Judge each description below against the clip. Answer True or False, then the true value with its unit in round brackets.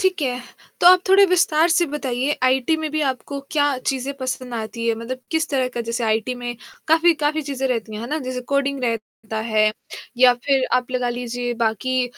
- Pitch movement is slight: False (3.7 semitones)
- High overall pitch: True (255 Hz)